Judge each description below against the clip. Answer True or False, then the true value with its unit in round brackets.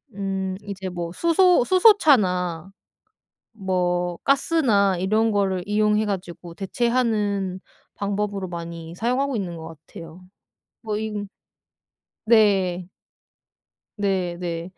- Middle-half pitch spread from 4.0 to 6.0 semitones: False (3.5 semitones)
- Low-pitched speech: False (195 Hz)